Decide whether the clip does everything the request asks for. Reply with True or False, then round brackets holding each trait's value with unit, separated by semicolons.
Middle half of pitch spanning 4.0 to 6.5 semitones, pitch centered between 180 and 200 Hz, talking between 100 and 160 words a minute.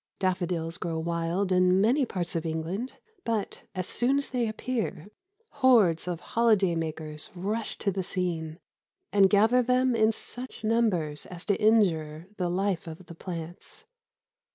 True (4.9 semitones; 185 Hz; 150 wpm)